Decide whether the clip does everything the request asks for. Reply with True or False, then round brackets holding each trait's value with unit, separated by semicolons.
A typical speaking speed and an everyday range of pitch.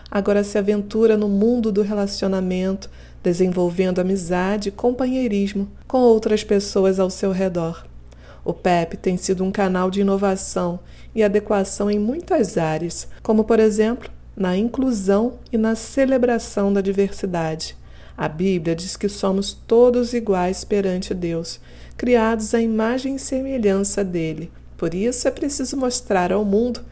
True (140 wpm; 3.3 semitones)